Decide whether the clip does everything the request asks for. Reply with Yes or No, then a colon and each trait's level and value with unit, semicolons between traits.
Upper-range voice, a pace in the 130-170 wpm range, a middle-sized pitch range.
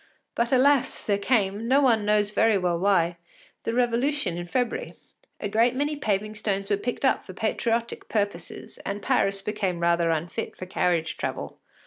Yes: high, 210 Hz; average, 165 wpm; average, 4.2 semitones